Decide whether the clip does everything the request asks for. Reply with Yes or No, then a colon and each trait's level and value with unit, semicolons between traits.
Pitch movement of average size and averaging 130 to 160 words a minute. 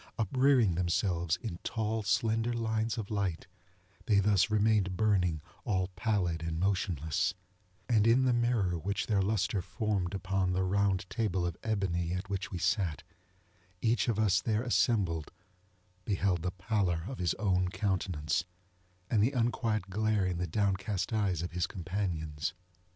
Yes: average, 3.4 semitones; average, 150 wpm